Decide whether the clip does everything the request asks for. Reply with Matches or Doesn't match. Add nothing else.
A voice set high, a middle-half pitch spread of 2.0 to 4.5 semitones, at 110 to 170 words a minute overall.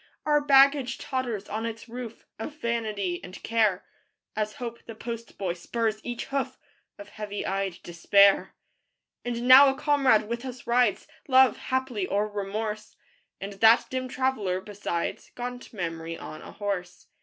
Matches